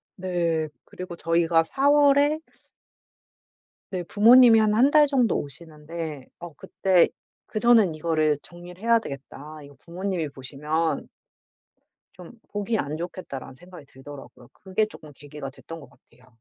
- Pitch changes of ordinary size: No, wide, 5.7 semitones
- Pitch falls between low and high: Yes, medium, 170 Hz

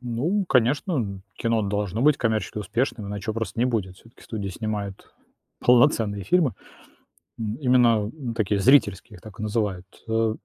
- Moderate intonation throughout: Yes, average, 3.2 semitones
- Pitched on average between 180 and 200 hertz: No, low, 110 Hz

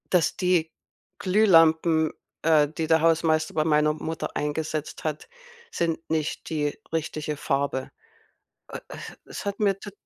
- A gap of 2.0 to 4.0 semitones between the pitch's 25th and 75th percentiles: No, narrow, 1.4 semitones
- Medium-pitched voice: Yes, medium, 160 Hz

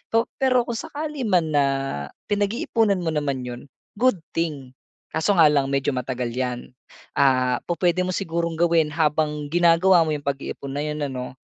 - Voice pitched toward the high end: No, medium, 155 Hz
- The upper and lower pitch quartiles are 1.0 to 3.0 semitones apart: No, average, 4.8 semitones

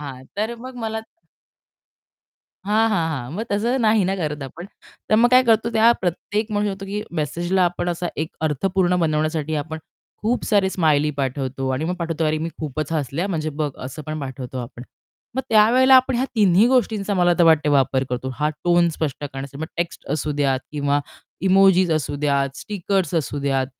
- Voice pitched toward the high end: No, medium, 165 Hz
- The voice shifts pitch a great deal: Yes, wide, 5.9 semitones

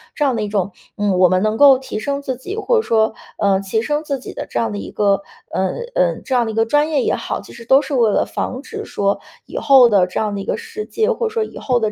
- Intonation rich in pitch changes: Yes, wide, 6.0 semitones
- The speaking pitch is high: Yes, high, 235 Hz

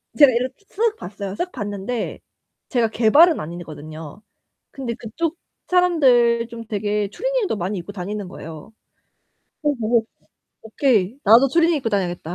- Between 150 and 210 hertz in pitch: No, high, 225 Hz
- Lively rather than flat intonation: Yes, wide, 5.7 semitones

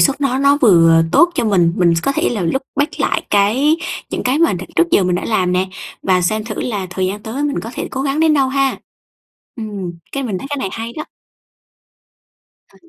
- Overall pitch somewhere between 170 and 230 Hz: Yes, high, 225 Hz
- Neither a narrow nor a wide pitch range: No, wide, 6.7 semitones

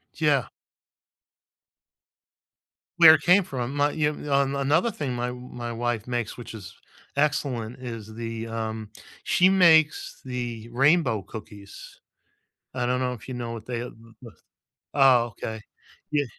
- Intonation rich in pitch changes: No, average, 3.8 semitones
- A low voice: Yes, low, 125 Hz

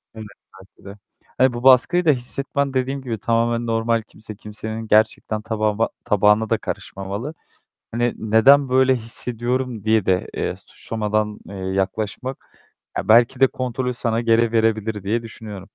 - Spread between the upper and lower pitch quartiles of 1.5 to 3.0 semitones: Yes, average, 2.7 semitones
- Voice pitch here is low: Yes, low, 115 Hz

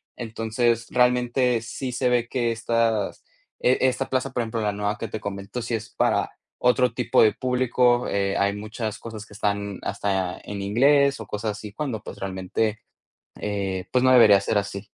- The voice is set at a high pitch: No, low, 115 Hz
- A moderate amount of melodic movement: Yes, average, 3.3 semitones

